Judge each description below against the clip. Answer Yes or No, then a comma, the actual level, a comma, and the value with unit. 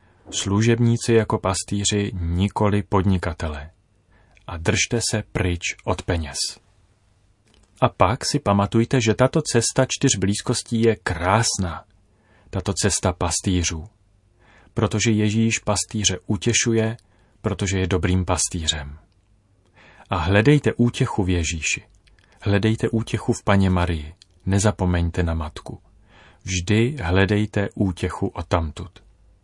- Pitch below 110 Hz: Yes, low, 100 Hz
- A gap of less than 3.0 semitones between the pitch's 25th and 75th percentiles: No, average, 3.3 semitones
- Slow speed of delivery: Yes, slow, 105 wpm